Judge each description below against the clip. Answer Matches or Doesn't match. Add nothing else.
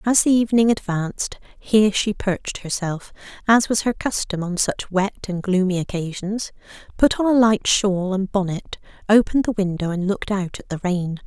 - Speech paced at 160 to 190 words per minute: Matches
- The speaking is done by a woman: Matches